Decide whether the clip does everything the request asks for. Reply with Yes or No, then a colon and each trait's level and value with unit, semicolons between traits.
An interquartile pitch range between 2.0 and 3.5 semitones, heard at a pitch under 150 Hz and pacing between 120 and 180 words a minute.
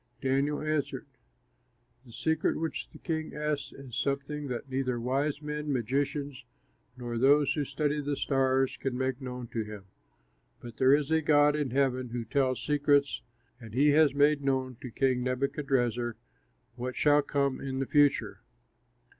Yes: narrow, 2.4 semitones; low, 135 Hz; average, 155 wpm